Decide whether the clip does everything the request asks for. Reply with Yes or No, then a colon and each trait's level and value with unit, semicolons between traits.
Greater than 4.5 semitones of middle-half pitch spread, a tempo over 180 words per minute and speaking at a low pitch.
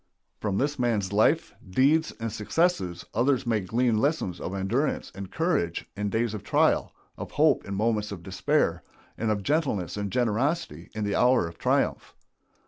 No: average, 4.9 semitones; average, 165 wpm; low, 110 Hz